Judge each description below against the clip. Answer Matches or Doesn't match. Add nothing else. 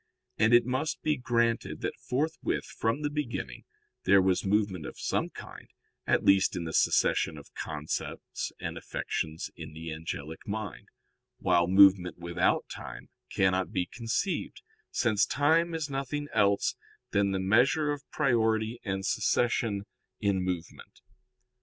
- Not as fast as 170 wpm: Matches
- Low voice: Matches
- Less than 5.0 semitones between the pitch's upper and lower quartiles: Doesn't match